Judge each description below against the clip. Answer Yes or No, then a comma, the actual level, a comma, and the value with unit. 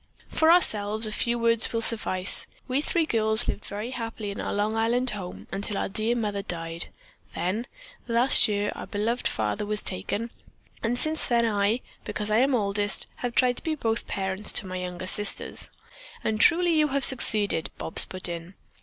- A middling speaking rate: Yes, average, 180 wpm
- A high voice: Yes, high, 215 Hz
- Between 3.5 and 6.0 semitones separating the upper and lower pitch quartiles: No, average, 3.0 semitones